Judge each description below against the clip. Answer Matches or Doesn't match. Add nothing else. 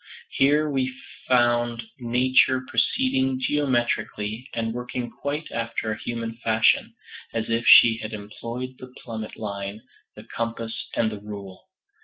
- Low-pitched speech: Matches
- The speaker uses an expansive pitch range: Doesn't match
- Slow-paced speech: Matches